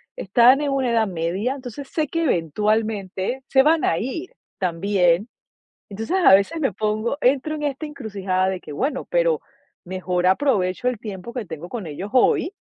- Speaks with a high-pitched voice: Yes, high, 220 Hz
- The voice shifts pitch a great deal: Yes, wide, 6.5 semitones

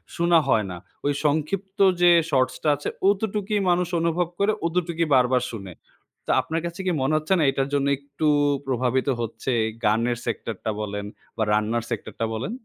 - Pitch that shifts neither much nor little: No, wide, 6.5 semitones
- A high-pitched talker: No, medium, 145 Hz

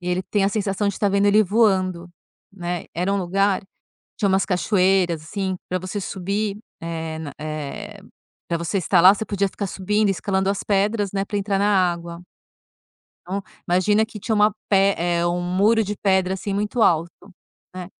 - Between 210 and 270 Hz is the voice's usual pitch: No, high, 195 Hz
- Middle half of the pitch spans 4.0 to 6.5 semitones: No, narrow, 2.4 semitones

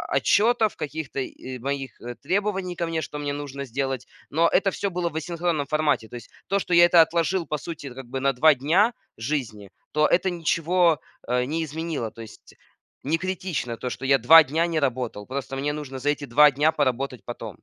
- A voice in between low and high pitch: Yes, medium, 150 Hz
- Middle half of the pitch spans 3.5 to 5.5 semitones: Yes, average, 4.2 semitones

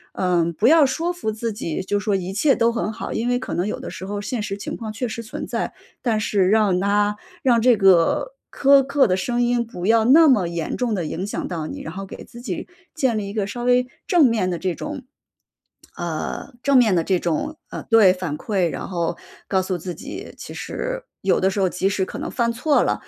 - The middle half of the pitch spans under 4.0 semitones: No, average, 4.8 semitones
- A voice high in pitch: Yes, high, 210 Hz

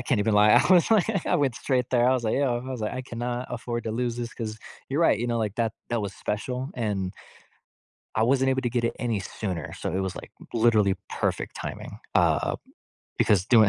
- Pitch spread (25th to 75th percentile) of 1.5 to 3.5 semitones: Yes, average, 2.9 semitones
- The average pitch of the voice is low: Yes, low, 120 Hz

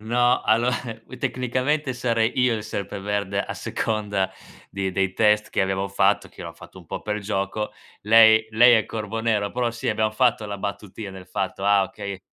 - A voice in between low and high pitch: No, low, 105 Hz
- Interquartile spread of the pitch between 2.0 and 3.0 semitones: Yes, narrow, 2.6 semitones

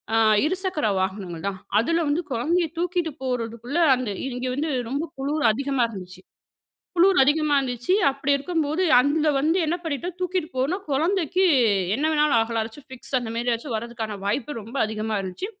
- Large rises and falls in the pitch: Yes, wide, 5.8 semitones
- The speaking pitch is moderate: No, very high, 275 Hz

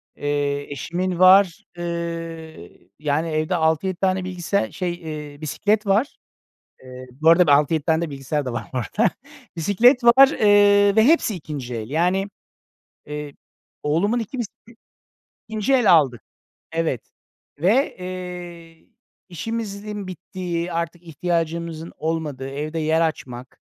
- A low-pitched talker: No, medium, 170 Hz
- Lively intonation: No, average, 4.1 semitones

